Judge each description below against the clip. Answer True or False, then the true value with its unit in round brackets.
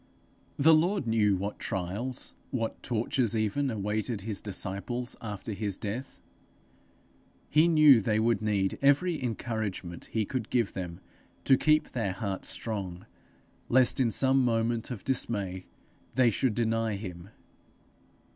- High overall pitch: False (115 Hz)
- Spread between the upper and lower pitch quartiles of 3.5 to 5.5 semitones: True (4.2 semitones)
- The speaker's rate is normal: False (130 wpm)